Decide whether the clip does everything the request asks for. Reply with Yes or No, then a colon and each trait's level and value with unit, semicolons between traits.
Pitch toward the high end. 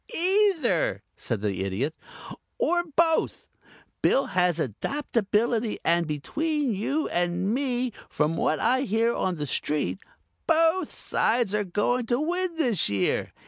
Yes: high, 235 Hz